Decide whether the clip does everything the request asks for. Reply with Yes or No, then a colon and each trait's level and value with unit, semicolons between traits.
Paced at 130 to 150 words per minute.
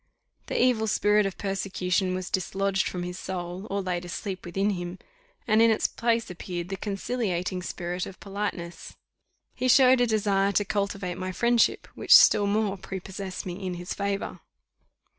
No: average, 160 wpm